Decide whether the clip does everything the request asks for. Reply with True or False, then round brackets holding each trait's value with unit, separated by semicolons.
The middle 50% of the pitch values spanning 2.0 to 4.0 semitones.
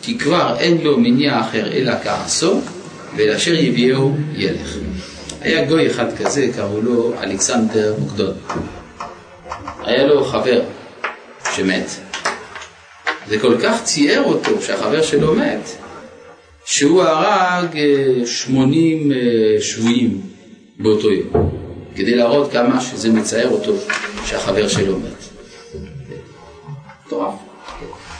False (5.4 semitones)